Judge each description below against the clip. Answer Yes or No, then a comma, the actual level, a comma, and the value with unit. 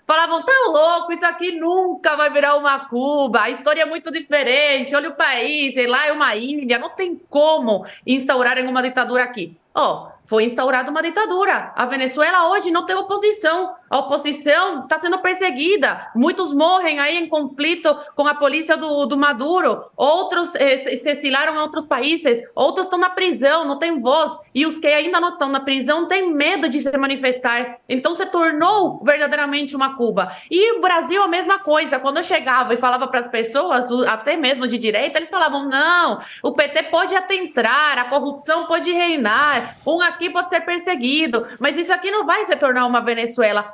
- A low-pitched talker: No, very high, 295 Hz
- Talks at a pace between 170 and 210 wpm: Yes, fast, 185 wpm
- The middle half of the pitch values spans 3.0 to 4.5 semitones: Yes, average, 4.1 semitones